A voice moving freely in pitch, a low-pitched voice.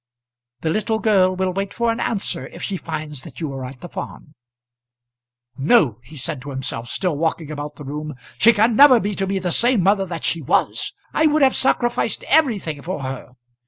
No: wide, 6.6 semitones; medium, 180 Hz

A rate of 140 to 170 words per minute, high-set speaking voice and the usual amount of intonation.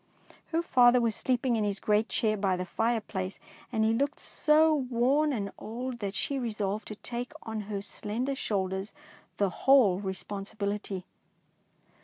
Yes: average, 160 wpm; high, 220 Hz; average, 3.8 semitones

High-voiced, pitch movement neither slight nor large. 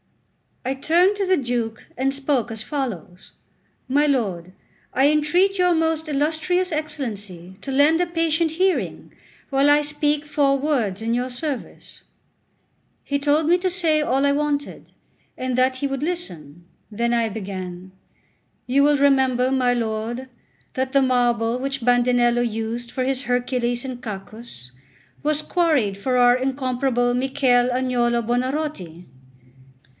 Yes: very high, 260 Hz; average, 3.8 semitones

